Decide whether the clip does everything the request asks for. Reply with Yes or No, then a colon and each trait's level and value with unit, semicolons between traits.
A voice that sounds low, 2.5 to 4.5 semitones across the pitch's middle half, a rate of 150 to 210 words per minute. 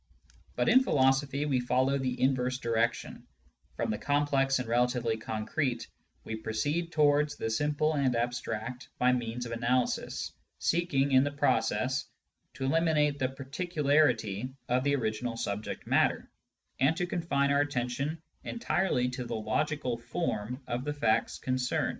No: low, 130 Hz; average, 3.5 semitones; average, 140 wpm